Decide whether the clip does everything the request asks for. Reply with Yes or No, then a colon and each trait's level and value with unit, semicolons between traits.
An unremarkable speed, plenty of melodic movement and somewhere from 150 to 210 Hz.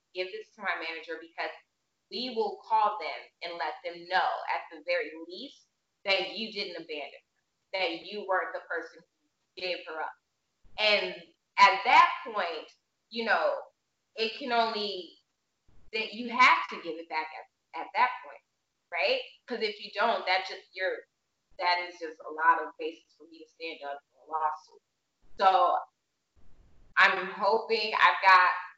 Yes: average, 165 wpm; wide, 5.7 semitones; high, 190 Hz